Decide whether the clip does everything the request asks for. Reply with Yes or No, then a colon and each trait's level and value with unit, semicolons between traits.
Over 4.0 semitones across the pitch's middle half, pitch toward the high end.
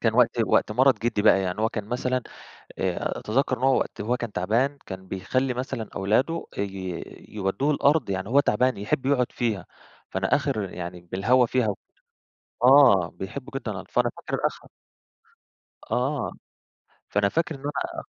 No: average, 4.8 semitones; low, 115 Hz